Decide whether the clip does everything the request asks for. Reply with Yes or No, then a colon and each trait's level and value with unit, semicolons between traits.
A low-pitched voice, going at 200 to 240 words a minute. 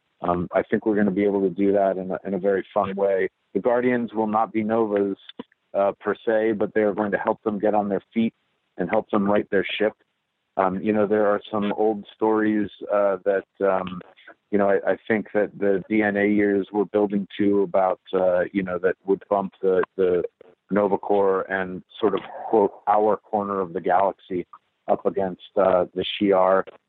Yes: low, 100 Hz; fast, 205 wpm